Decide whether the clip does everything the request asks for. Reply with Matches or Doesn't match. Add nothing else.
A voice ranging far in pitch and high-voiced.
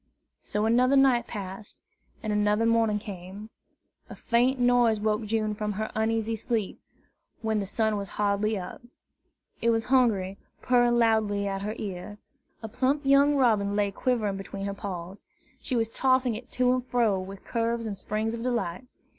Doesn't match